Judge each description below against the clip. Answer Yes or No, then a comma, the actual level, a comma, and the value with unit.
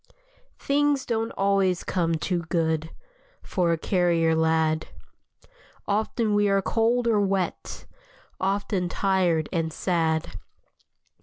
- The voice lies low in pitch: No, medium, 185 Hz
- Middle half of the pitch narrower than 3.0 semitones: No, average, 4.0 semitones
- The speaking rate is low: Yes, slow, 105 wpm